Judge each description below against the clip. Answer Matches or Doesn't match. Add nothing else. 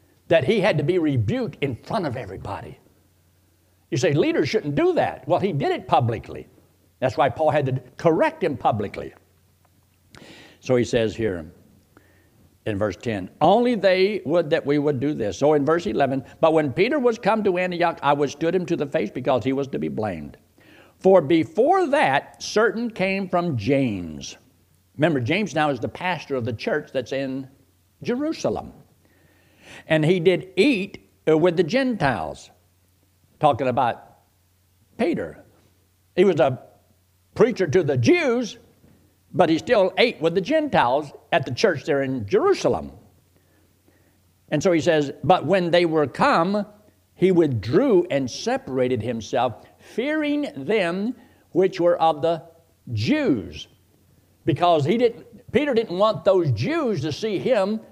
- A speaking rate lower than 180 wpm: Matches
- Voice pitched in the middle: Matches